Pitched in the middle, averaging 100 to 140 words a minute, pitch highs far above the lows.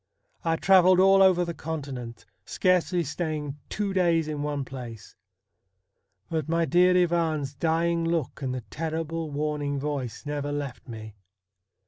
No: medium, 155 Hz; slow, 135 wpm; average, 3.1 semitones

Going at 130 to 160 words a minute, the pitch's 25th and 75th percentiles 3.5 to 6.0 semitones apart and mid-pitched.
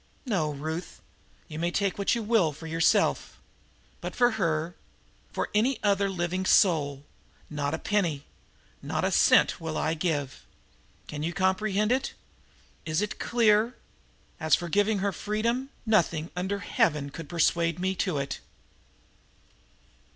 Yes: average, 140 wpm; average, 4.7 semitones; medium, 180 Hz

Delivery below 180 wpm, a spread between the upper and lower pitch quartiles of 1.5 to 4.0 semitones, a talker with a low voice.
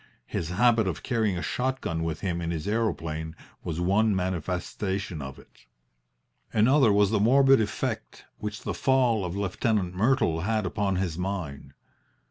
No: average, 155 wpm; average, 4.4 semitones; very low, 95 Hz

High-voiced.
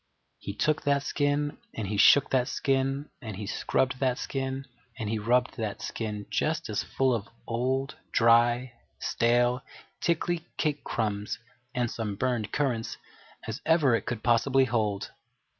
No: low, 125 Hz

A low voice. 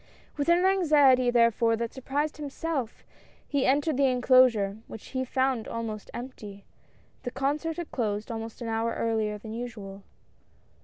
No: high, 245 Hz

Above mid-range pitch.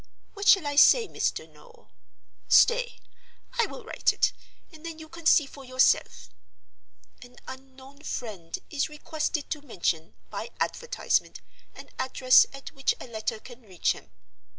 Yes: very high, 275 Hz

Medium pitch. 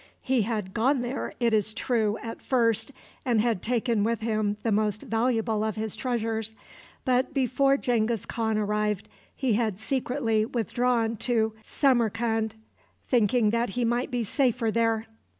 No: high, 225 Hz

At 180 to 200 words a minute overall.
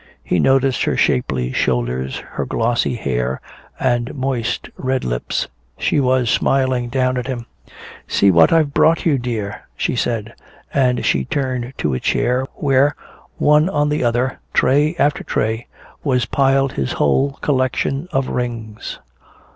No: average, 145 wpm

